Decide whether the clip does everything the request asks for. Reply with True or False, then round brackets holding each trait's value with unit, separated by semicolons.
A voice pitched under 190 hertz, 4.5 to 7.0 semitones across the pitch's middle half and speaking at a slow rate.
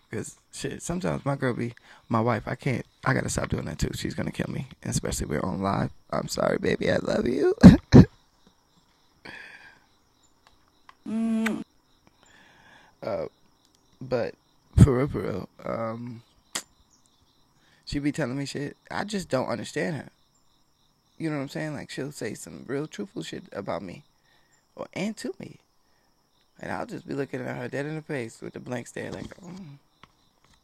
False (140 Hz; 5.2 semitones; 170 wpm)